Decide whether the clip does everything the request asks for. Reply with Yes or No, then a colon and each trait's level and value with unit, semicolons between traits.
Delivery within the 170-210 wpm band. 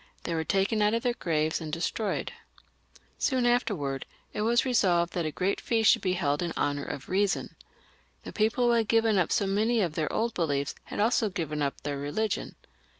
Yes: average, 200 wpm